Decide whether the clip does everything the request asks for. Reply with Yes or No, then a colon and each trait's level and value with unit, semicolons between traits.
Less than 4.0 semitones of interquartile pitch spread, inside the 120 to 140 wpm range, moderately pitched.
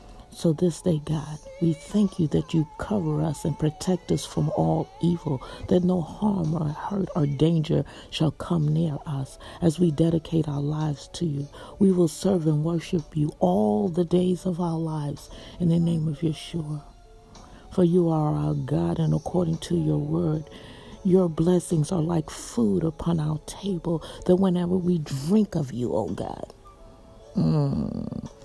No: average, 2.9 semitones; average, 170 wpm; medium, 165 Hz